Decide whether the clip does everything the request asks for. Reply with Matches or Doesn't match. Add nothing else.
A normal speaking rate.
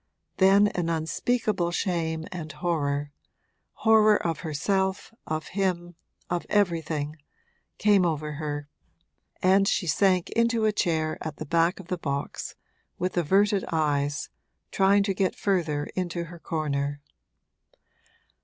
Doesn't match